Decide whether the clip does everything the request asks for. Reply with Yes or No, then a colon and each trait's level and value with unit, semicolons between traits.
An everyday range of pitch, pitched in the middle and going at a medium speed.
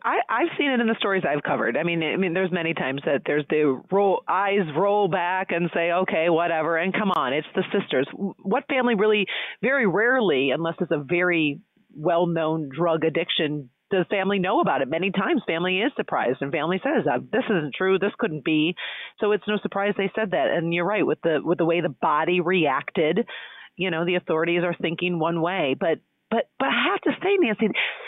No: average, 3.5 semitones; medium, 180 Hz; fast, 210 wpm